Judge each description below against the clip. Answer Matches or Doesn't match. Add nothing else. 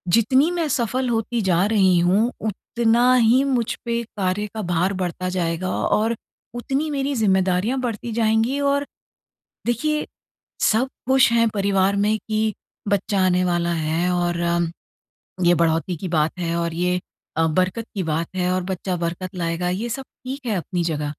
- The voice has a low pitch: Doesn't match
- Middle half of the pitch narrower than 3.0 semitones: Doesn't match